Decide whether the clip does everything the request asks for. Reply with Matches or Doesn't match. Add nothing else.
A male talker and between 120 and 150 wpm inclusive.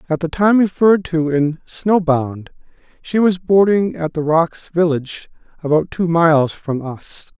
Doesn't match